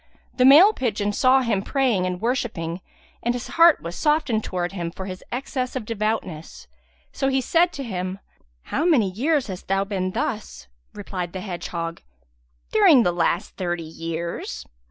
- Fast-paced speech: No, average, 160 wpm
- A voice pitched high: Yes, high, 205 Hz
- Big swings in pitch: Yes, wide, 6.5 semitones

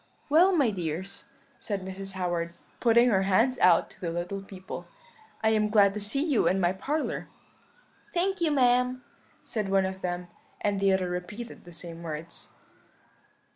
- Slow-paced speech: No, average, 165 wpm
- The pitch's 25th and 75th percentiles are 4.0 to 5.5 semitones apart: Yes, average, 5.1 semitones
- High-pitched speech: Yes, high, 195 Hz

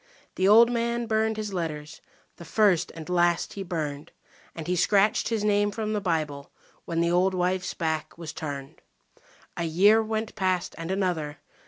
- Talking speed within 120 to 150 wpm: No, average, 170 wpm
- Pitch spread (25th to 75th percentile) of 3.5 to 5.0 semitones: Yes, average, 4.3 semitones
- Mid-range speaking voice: Yes, medium, 180 Hz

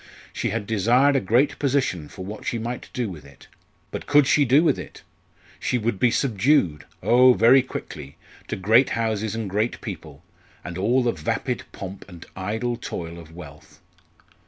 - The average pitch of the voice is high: No, low, 110 Hz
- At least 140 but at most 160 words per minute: No, average, 175 wpm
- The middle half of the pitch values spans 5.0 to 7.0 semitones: Yes, average, 5.3 semitones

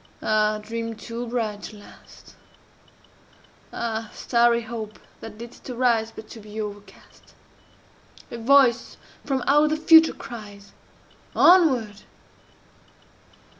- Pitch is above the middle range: Yes, high, 230 Hz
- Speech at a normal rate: No, slow, 105 wpm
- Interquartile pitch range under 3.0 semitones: Yes, narrow, 2.4 semitones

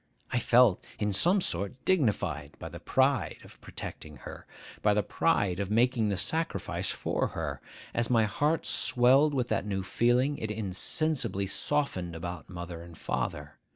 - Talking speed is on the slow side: No, average, 155 wpm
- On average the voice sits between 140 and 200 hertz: No, low, 105 Hz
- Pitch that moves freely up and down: Yes, wide, 6.3 semitones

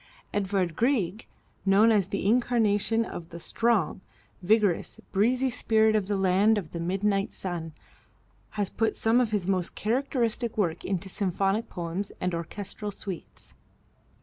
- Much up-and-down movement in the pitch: No, average, 3.3 semitones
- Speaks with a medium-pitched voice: No, high, 200 Hz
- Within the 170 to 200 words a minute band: No, average, 140 wpm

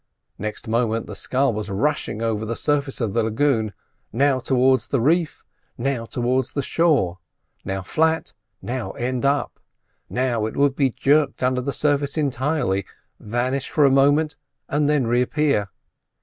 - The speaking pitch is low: Yes, low, 130 Hz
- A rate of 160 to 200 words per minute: No, average, 150 wpm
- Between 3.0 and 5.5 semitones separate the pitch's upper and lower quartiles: Yes, average, 3.8 semitones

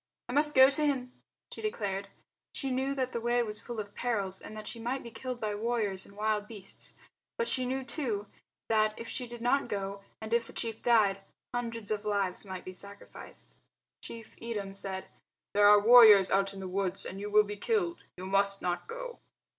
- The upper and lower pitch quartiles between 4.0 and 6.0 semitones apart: No, average, 3.6 semitones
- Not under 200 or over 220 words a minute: Yes, fast, 205 wpm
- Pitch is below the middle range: No, high, 215 Hz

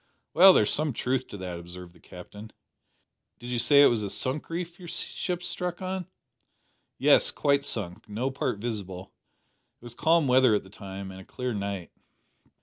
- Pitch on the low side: Yes, low, 120 Hz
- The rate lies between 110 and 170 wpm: No, average, 180 wpm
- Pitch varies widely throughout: Yes, wide, 7.6 semitones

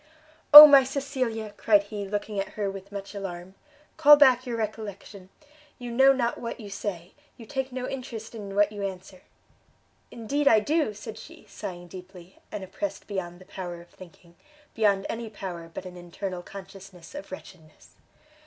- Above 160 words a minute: Yes, average, 170 wpm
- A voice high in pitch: Yes, high, 205 Hz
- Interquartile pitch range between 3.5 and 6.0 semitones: Yes, average, 3.9 semitones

